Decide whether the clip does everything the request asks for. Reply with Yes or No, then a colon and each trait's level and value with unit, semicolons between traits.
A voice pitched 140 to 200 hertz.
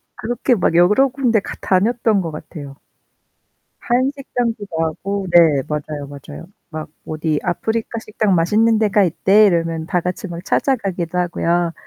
Yes: medium, 185 Hz